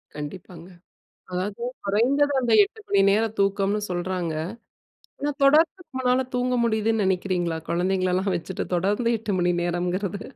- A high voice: Yes, high, 200 Hz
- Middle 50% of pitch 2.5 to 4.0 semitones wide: No, average, 4.6 semitones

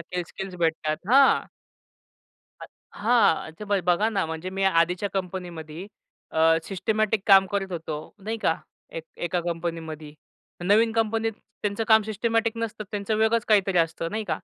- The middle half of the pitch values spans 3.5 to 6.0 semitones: Yes, average, 4.5 semitones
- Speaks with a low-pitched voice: No, high, 195 Hz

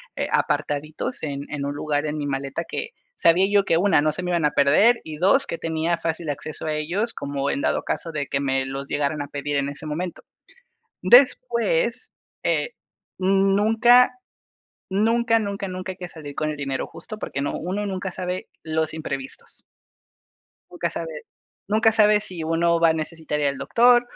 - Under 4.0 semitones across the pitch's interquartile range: No, average, 5.1 semitones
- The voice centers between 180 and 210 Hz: No, medium, 165 Hz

